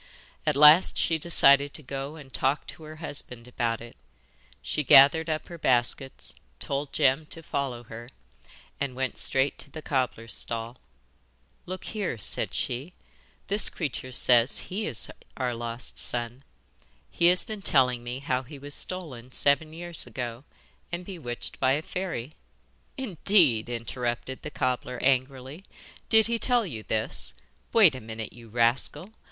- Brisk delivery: No, average, 150 wpm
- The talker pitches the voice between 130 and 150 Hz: Yes, low, 135 Hz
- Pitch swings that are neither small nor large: Yes, average, 4.7 semitones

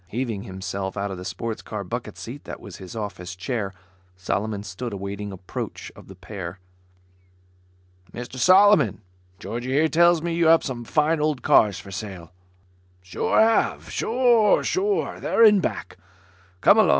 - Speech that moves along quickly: No, average, 155 wpm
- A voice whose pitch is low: Yes, low, 110 Hz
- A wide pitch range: Yes, wide, 9.0 semitones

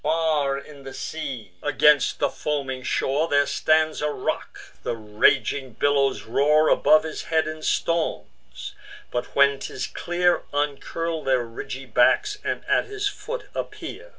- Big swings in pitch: No, average, 3.1 semitones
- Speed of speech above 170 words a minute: No, average, 145 wpm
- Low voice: No, medium, 145 Hz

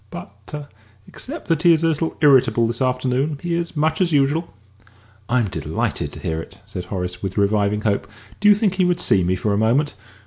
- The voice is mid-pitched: No, low, 130 Hz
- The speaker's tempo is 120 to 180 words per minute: No, fast, 205 wpm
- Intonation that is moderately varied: No, wide, 8.1 semitones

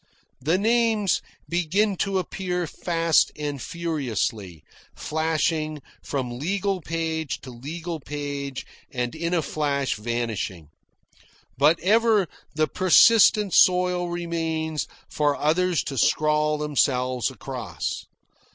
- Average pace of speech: No, slow, 105 wpm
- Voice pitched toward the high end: No, medium, 155 Hz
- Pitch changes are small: No, average, 4.2 semitones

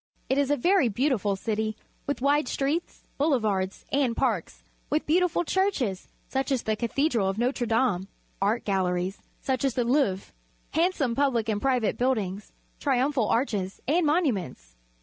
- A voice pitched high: Yes, high, 245 Hz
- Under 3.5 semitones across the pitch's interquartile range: No, wide, 5.5 semitones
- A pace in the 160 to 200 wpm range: No, average, 150 wpm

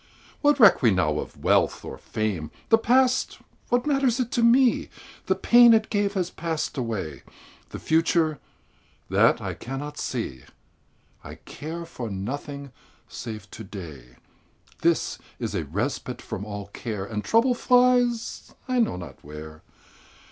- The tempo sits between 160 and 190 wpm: No, average, 145 wpm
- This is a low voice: No, medium, 145 Hz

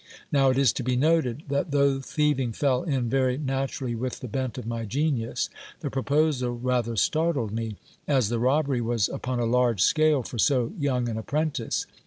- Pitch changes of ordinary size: Yes, average, 3.1 semitones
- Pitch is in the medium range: No, low, 130 Hz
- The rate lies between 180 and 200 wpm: Yes, average, 185 wpm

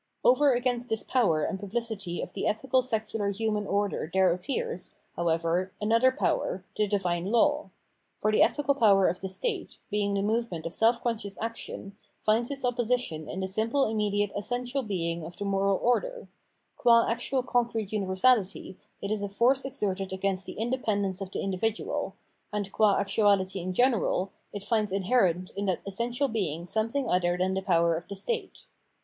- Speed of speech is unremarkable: Yes, average, 175 wpm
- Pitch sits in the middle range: No, high, 205 Hz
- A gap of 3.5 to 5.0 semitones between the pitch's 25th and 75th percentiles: Yes, average, 4.0 semitones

